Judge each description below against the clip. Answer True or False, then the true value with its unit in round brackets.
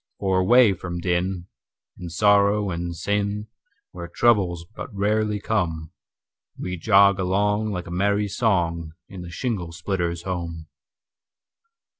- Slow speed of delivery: True (110 wpm)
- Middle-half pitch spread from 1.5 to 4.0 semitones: True (3.1 semitones)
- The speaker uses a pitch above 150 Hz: False (95 Hz)